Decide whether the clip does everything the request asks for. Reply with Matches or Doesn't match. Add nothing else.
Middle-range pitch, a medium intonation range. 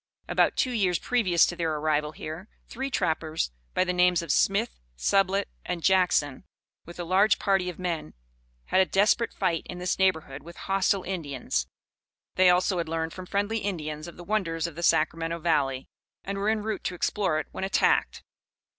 Matches